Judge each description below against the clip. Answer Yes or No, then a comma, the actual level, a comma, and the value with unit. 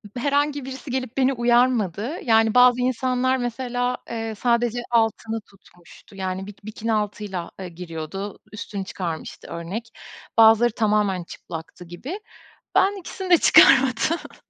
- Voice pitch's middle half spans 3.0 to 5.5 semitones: Yes, average, 4.3 semitones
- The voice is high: Yes, high, 225 Hz